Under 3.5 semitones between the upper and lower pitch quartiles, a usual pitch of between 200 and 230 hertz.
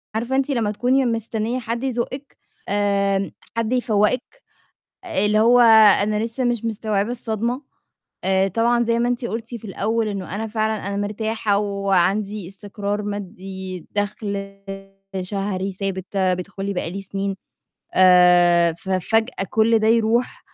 Yes: average, 2.8 semitones; high, 210 Hz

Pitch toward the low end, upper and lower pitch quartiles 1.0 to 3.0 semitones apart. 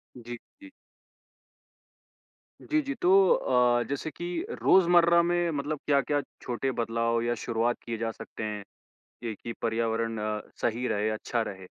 No: low, 120 Hz; average, 5.1 semitones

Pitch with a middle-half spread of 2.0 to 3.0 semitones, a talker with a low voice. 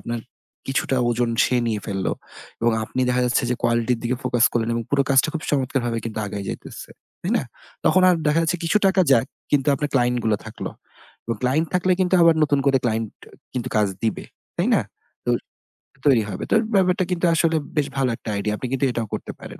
No: average, 4.4 semitones; low, 125 Hz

